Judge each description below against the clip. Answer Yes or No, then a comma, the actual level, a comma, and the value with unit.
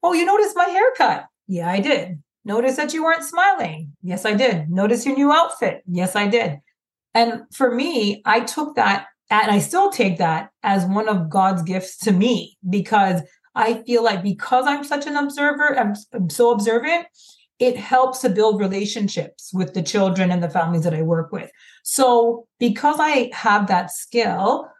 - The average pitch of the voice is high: Yes, high, 220 Hz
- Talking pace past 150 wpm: Yes, average, 180 wpm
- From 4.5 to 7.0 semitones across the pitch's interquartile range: Yes, wide, 5.6 semitones